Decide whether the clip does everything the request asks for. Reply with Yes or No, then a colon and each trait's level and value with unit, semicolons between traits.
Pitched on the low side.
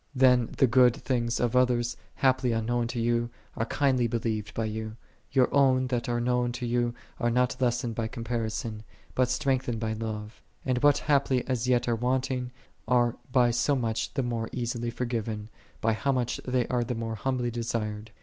Yes: low, 120 Hz